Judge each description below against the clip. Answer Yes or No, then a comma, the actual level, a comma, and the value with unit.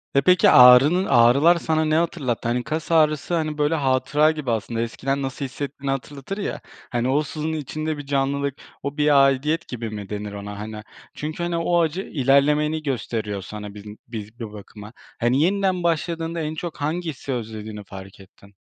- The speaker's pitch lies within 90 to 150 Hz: Yes, medium, 140 Hz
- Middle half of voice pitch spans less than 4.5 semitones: No, average, 5.2 semitones